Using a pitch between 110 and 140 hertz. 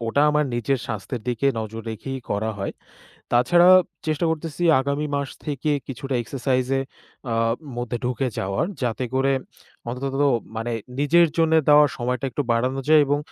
Yes: low, 135 Hz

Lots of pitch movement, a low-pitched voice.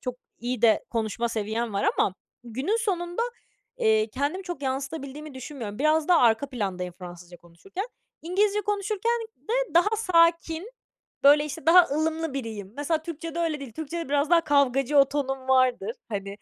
No: wide, 6.2 semitones; very high, 285 Hz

